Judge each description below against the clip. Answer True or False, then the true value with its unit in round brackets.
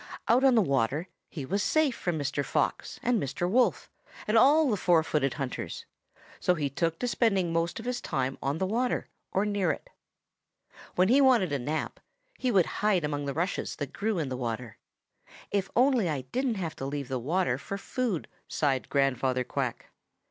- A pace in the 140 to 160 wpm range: False (190 wpm)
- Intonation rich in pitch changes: True (7.9 semitones)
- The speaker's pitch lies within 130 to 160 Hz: False (175 Hz)